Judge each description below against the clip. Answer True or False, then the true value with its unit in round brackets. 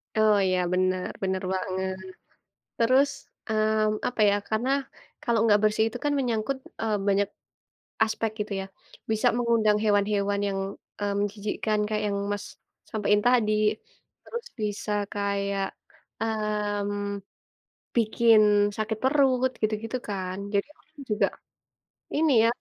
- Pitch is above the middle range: True (215 Hz)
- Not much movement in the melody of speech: True (1.9 semitones)